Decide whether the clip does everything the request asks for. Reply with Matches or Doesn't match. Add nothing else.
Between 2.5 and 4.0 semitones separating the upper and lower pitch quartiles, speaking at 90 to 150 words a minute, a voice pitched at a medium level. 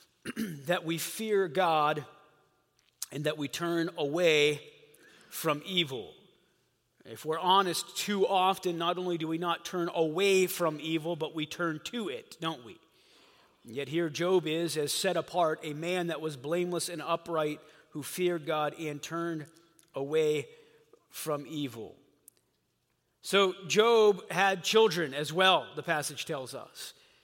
Matches